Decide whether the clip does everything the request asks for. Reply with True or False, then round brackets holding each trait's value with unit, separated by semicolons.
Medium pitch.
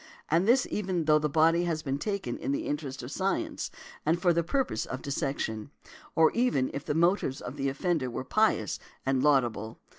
True (150 Hz)